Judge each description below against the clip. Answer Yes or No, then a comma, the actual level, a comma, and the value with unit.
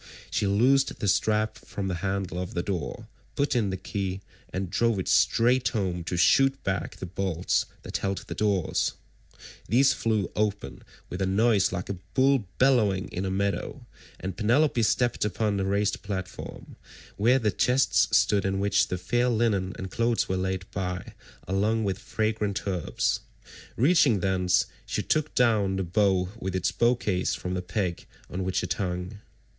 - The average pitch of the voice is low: Yes, low, 100 Hz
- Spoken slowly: No, average, 170 wpm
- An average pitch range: Yes, average, 3.3 semitones